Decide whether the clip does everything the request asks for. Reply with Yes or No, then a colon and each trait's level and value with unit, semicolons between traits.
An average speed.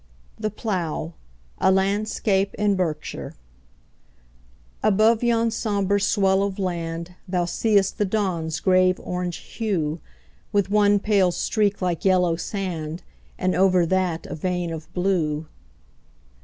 No: slow, 120 wpm